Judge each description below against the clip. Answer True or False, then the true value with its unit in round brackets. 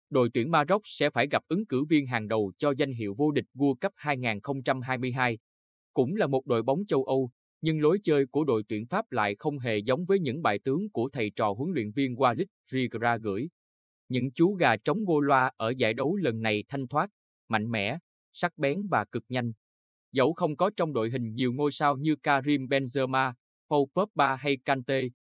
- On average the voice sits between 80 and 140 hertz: True (135 Hz)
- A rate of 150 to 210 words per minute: True (205 wpm)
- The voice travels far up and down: False (4.2 semitones)